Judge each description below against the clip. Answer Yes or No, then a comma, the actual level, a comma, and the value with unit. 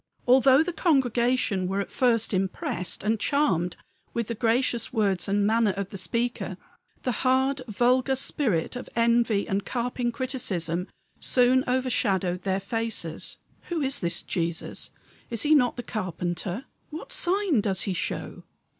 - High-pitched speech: Yes, high, 230 Hz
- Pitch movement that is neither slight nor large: Yes, average, 4.9 semitones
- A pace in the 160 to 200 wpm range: No, average, 145 wpm